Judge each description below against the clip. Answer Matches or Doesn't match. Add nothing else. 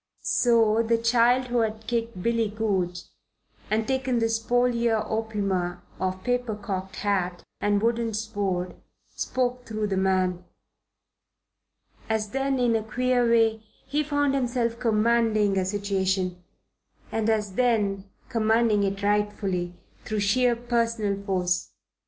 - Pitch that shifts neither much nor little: Matches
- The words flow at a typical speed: Doesn't match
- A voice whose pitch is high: Matches